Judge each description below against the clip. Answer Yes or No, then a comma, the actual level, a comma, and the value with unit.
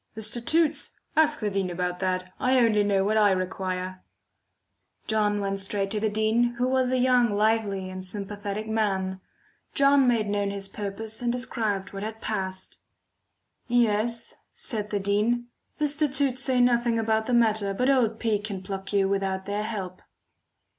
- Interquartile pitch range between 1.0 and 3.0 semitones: No, average, 3.4 semitones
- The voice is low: No, high, 215 Hz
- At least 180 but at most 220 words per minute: No, average, 165 wpm